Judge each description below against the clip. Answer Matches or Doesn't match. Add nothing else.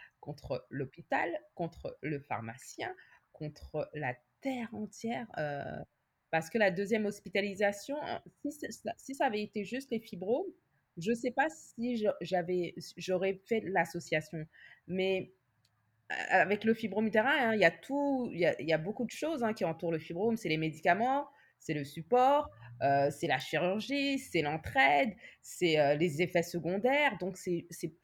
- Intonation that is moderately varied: Doesn't match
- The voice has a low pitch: Doesn't match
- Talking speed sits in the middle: Matches